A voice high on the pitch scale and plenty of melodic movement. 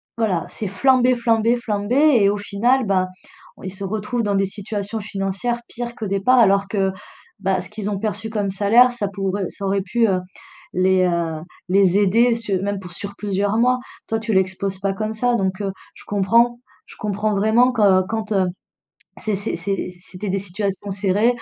No: high, 205 Hz; narrow, 2.6 semitones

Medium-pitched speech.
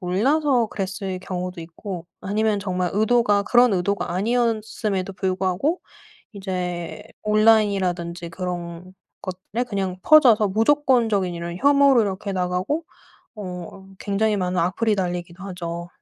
No: high, 195 Hz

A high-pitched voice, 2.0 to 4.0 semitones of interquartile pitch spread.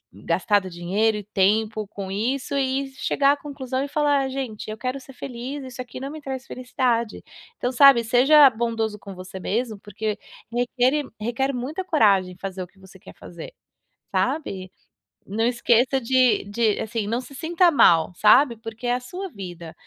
No: high, 235 Hz; average, 4.5 semitones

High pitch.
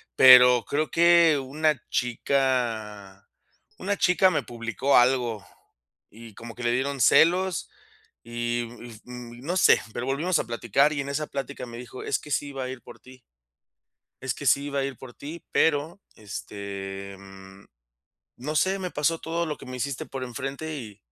No: low, 130 Hz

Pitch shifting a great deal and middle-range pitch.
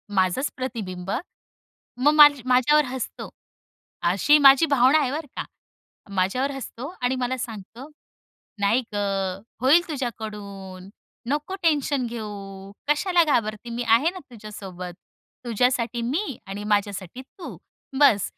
No: wide, 5.8 semitones; high, 245 Hz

